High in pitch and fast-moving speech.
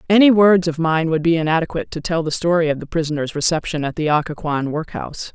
No: medium, 160 Hz; fast, 215 wpm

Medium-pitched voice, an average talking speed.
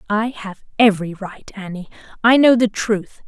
No: high, 205 Hz; average, 165 wpm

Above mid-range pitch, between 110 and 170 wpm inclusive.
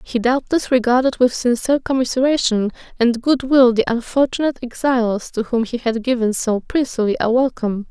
Yes: high, 245 Hz; average, 160 wpm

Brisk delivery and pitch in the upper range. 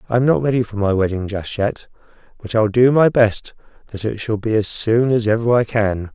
No: fast, 235 wpm; low, 110 Hz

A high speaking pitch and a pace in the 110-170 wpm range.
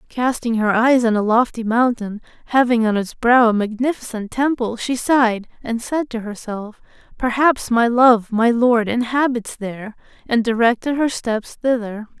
Yes: high, 235 Hz; average, 155 wpm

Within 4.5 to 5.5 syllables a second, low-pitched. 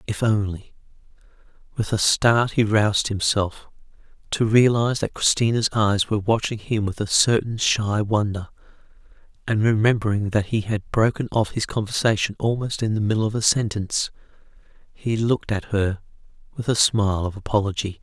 Yes: 5.3 syllables/s; low, 105 Hz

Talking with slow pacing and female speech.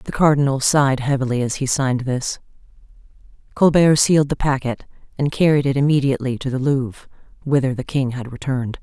No: average, 165 wpm; female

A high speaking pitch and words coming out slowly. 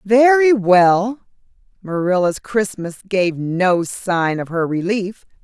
Yes: high, 195 Hz; slow, 110 wpm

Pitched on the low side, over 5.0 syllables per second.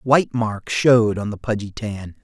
No: low, 110 Hz; 4.6 syllables/s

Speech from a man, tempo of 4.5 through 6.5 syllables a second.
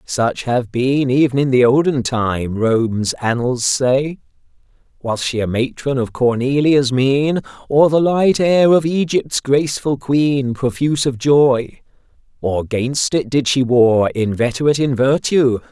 No: male; 4.0 syllables/s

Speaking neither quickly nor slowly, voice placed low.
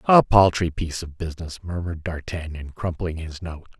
Yes: average, 160 wpm; very low, 85 Hz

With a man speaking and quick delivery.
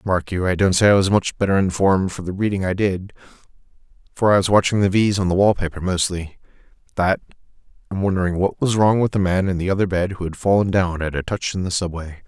Yes: male; fast, 230 wpm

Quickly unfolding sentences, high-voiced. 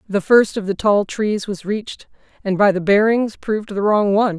Yes: fast, 220 wpm; high, 205 Hz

